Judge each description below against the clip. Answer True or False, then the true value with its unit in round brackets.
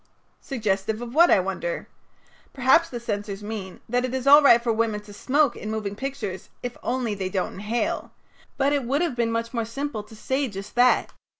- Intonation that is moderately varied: True (4.1 semitones)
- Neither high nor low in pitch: False (235 Hz)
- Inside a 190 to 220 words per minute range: True (205 wpm)